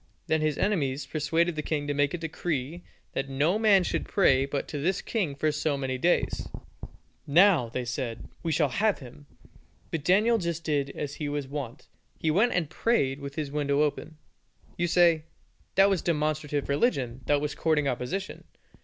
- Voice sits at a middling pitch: Yes, medium, 150 Hz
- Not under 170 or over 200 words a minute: Yes, average, 180 wpm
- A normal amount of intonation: Yes, average, 3.7 semitones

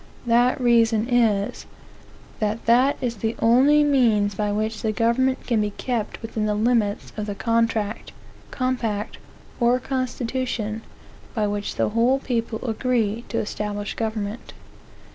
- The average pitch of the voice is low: No, high, 230 Hz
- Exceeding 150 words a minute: No, slow, 135 wpm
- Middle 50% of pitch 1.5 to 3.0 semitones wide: Yes, narrow, 2.6 semitones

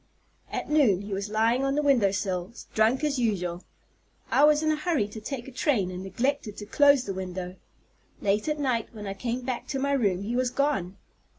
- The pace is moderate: No, fast, 210 wpm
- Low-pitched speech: No, high, 230 Hz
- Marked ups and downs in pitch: Yes, wide, 5.9 semitones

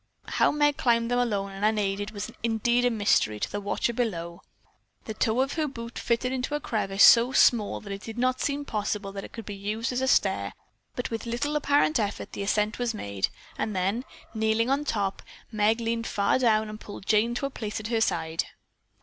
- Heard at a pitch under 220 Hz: No, high, 225 Hz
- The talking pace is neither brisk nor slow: No, fast, 215 wpm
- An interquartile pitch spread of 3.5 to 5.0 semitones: No, average, 3.1 semitones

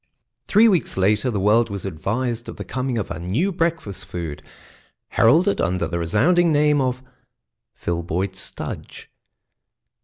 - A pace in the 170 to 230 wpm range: No, average, 140 wpm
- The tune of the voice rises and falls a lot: Yes, wide, 8.2 semitones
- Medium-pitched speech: No, low, 115 Hz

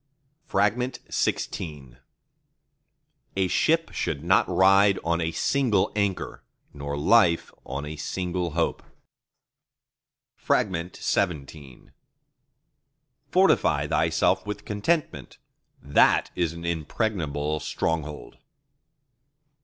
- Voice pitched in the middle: No, very low, 85 Hz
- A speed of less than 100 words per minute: Yes, slow, 80 wpm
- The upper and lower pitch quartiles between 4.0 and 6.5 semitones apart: Yes, average, 4.9 semitones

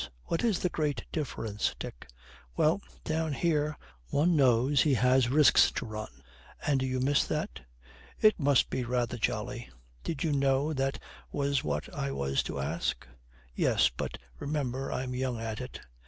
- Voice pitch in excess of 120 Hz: Yes, low, 135 Hz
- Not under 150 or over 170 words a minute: Yes, average, 155 wpm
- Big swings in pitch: No, average, 3.7 semitones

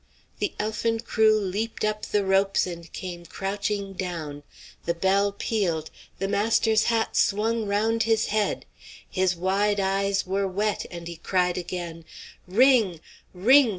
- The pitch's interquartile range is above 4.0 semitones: No, average, 2.9 semitones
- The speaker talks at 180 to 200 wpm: No, average, 140 wpm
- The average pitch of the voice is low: No, high, 200 Hz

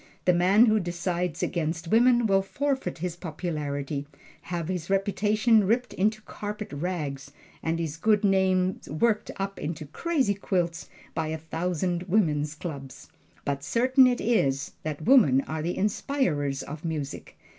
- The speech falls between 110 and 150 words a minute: Yes, average, 145 wpm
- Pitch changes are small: No, average, 5.2 semitones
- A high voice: No, medium, 180 Hz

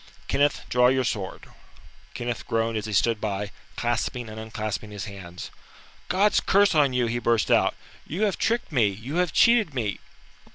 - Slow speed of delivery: No, average, 170 wpm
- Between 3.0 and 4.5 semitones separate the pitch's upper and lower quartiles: No, average, 5.2 semitones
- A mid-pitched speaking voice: No, low, 120 Hz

